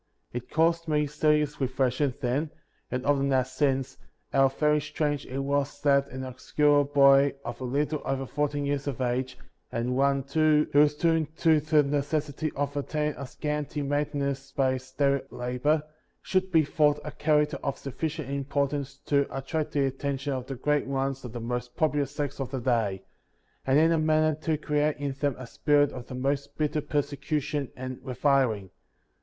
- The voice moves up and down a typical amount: No, narrow, 2.0 semitones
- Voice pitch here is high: No, medium, 140 Hz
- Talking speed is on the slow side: No, average, 180 wpm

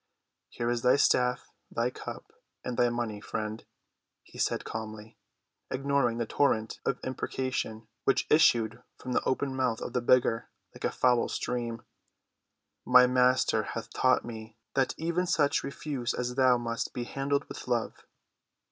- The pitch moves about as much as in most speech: No, narrow, 2.1 semitones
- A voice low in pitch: Yes, low, 125 Hz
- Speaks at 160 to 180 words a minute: No, average, 150 wpm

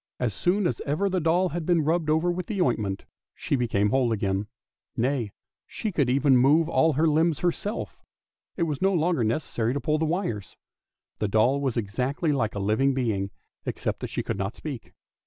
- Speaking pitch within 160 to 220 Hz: No, medium, 140 Hz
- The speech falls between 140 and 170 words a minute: No, average, 195 wpm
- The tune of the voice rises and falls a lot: Yes, wide, 6.4 semitones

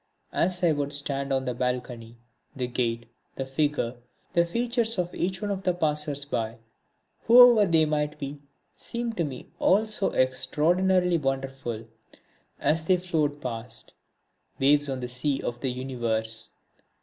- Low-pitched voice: No, medium, 145 Hz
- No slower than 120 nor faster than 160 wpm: Yes, average, 150 wpm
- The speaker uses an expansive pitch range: Yes, wide, 5.8 semitones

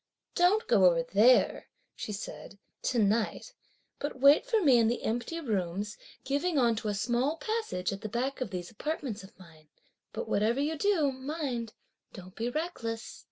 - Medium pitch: No, high, 240 Hz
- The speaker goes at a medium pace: Yes, average, 170 wpm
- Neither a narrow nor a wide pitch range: No, wide, 6.2 semitones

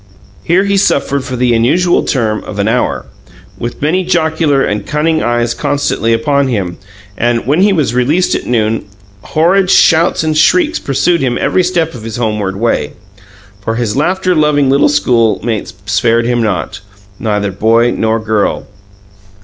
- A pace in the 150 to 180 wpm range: Yes, average, 155 wpm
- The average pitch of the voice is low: Yes, low, 125 Hz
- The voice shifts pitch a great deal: Yes, wide, 5.9 semitones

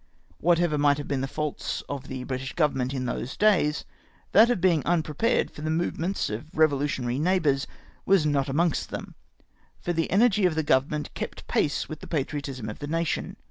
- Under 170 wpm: No, average, 180 wpm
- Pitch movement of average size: Yes, average, 3.8 semitones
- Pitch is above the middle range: No, medium, 150 Hz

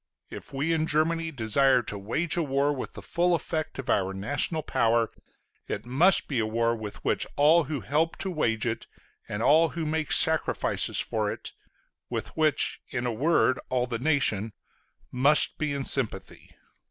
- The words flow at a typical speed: Yes, average, 175 wpm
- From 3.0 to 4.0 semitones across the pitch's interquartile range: No, average, 5.3 semitones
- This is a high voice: No, medium, 140 Hz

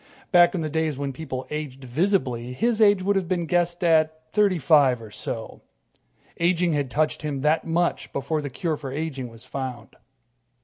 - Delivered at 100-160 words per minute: No, average, 180 wpm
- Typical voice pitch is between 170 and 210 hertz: No, medium, 155 Hz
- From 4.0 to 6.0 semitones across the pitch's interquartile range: Yes, average, 4.4 semitones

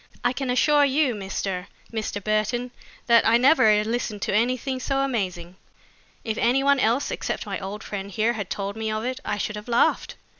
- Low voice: No, high, 225 Hz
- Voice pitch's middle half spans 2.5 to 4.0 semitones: Yes, average, 3.5 semitones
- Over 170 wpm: Yes, average, 190 wpm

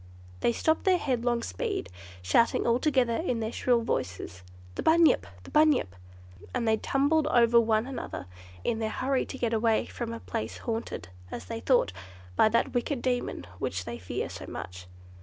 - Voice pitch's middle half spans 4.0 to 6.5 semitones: No, average, 3.1 semitones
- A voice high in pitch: Yes, high, 235 Hz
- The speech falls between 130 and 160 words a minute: No, average, 175 wpm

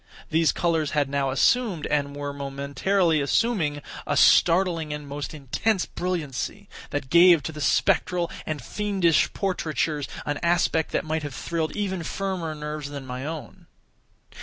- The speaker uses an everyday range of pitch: Yes, average, 3.5 semitones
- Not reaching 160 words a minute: Yes, average, 145 wpm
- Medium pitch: Yes, medium, 155 Hz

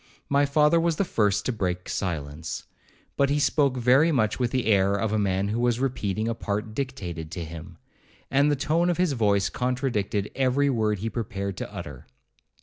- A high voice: No, low, 115 Hz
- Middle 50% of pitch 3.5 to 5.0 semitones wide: No, wide, 5.6 semitones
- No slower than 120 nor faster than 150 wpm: No, average, 190 wpm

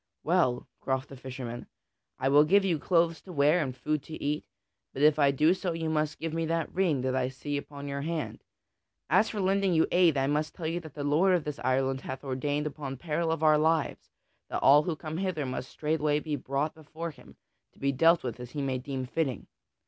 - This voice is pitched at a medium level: Yes, medium, 150 Hz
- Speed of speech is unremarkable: No, fast, 225 wpm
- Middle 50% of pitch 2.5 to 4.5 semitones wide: Yes, average, 3.2 semitones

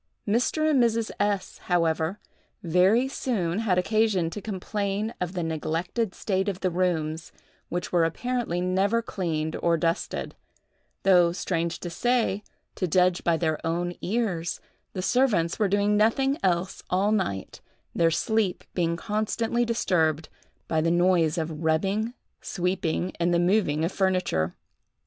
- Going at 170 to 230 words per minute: No, average, 140 wpm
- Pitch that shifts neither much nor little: Yes, average, 3.9 semitones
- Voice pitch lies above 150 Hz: Yes, medium, 185 Hz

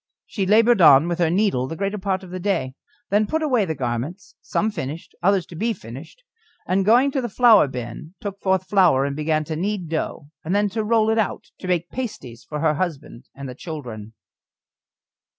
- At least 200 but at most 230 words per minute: Yes, fast, 205 wpm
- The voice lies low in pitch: No, medium, 185 Hz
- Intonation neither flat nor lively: No, wide, 5.7 semitones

